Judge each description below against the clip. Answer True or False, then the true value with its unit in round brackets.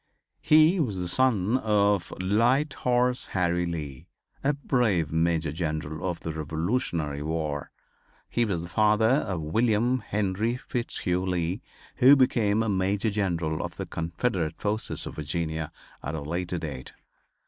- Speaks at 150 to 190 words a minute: False (140 wpm)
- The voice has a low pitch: True (95 Hz)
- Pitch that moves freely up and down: True (6.0 semitones)